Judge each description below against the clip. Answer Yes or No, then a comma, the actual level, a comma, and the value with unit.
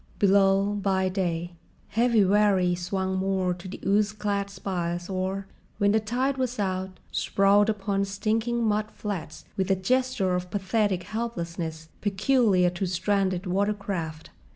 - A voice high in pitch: Yes, high, 195 Hz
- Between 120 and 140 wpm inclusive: Yes, slow, 135 wpm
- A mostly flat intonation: Yes, narrow, 2.2 semitones